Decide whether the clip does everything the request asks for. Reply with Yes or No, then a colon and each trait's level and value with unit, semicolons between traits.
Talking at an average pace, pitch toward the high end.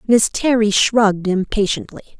No: slow, 110 wpm; high, 210 Hz